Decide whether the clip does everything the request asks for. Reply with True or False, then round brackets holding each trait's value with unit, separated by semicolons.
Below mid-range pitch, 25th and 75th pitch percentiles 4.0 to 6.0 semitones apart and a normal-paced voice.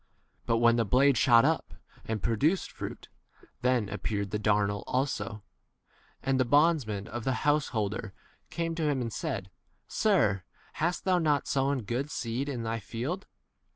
True (120 Hz; 5.1 semitones; 160 wpm)